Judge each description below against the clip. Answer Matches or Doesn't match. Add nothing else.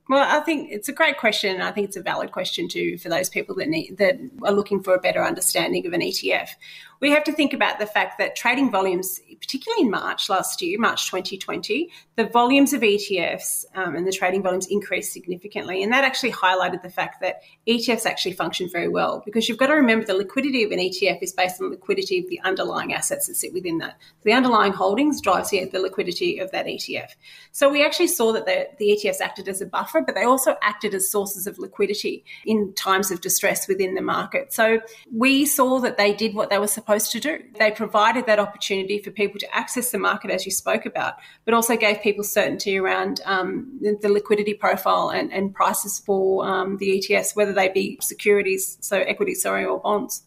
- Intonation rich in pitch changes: Matches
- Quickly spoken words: Matches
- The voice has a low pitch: Doesn't match